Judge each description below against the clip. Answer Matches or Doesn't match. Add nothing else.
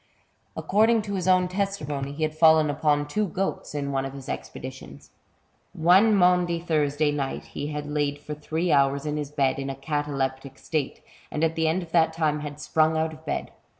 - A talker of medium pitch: Matches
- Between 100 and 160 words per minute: Doesn't match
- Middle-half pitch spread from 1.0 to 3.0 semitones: Matches